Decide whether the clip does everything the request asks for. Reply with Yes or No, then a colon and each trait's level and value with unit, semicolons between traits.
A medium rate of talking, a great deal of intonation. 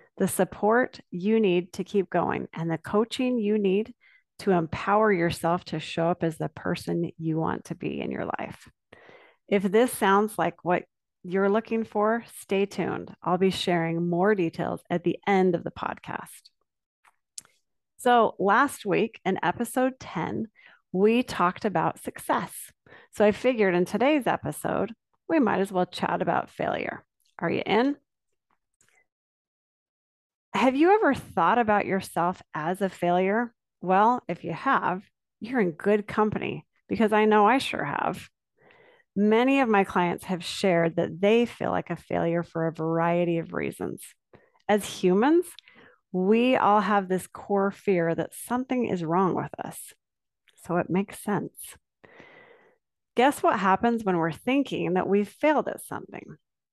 No: average, 150 wpm; average, 4.7 semitones